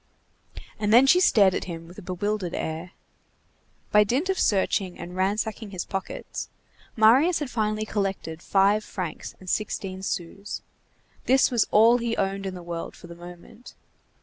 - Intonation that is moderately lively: Yes, average, 3.4 semitones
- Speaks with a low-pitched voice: No, high, 200 Hz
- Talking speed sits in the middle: Yes, average, 155 wpm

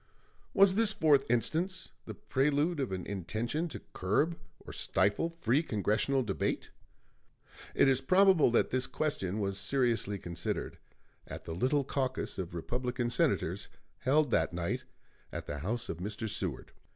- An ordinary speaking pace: Yes, average, 145 wpm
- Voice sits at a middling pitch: No, low, 125 Hz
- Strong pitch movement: Yes, wide, 6.8 semitones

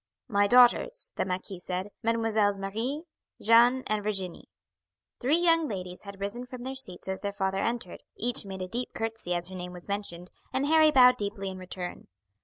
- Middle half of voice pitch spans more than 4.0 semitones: Yes, average, 4.7 semitones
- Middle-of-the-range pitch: No, high, 205 Hz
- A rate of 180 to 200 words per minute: Yes, average, 185 wpm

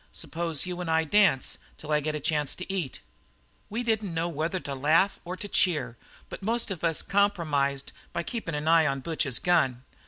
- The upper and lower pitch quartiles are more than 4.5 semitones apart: No, average, 3.9 semitones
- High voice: No, medium, 165 Hz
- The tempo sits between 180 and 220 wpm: Yes, average, 195 wpm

